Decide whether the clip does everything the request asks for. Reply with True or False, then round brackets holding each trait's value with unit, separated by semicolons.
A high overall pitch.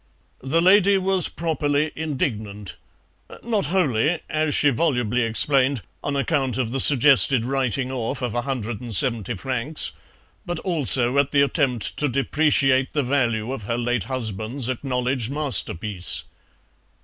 False (135 Hz)